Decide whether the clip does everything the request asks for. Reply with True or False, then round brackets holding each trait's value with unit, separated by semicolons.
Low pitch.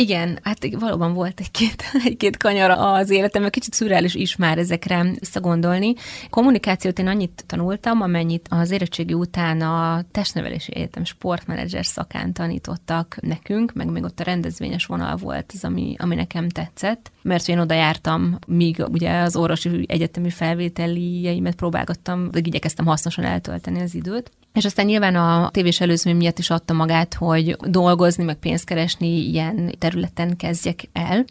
False (175 Hz)